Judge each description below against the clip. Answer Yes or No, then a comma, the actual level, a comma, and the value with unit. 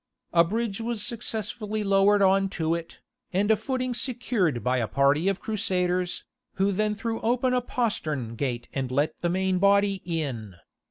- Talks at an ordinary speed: Yes, average, 165 wpm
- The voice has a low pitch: No, high, 195 Hz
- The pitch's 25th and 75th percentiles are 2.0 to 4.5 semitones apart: No, average, 5.1 semitones